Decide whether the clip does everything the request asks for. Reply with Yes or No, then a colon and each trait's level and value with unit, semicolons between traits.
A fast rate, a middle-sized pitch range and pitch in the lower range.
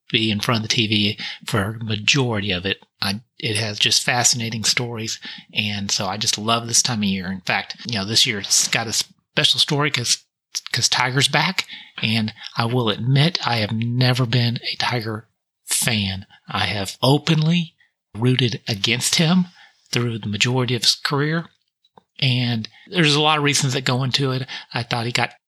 No: average, 180 wpm; average, 4.0 semitones; low, 120 Hz